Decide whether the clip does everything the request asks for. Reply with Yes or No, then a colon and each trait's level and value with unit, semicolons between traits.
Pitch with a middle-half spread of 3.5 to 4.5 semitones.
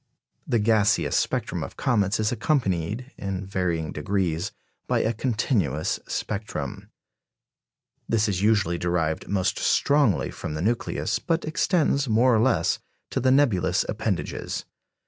No: average, 5.0 semitones